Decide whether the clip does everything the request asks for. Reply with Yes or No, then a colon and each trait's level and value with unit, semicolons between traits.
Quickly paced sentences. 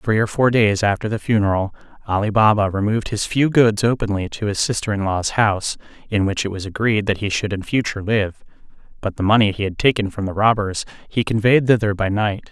Yes: fast, 215 wpm